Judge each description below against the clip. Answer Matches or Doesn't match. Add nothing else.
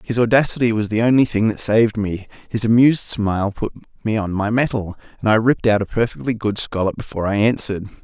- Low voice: Matches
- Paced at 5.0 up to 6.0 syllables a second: Doesn't match